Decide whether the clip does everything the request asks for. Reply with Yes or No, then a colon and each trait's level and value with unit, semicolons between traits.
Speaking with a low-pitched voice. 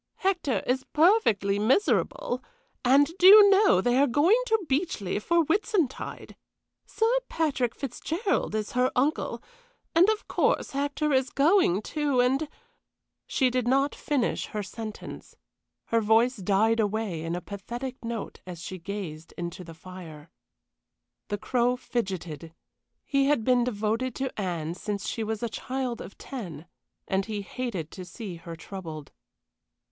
No: high, 235 Hz